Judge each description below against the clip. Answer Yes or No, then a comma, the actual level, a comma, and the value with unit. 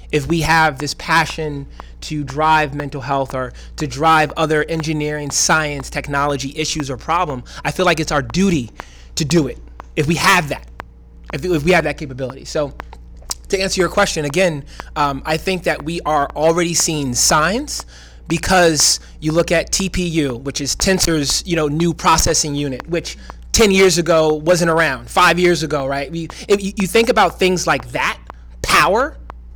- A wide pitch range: No, average, 3.4 semitones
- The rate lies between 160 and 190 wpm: Yes, average, 170 wpm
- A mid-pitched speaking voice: Yes, medium, 155 Hz